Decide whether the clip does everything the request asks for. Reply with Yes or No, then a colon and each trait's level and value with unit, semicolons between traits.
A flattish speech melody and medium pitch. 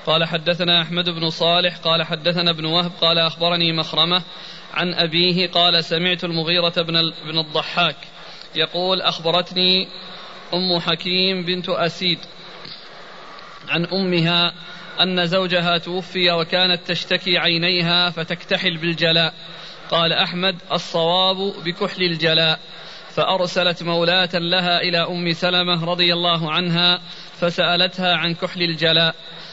Yes: narrow, 1.2 semitones; medium, 175 Hz